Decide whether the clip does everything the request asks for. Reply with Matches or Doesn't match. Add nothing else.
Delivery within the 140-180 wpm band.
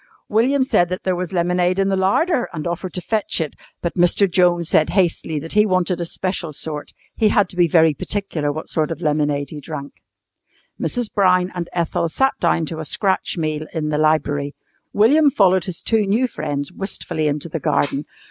Doesn't match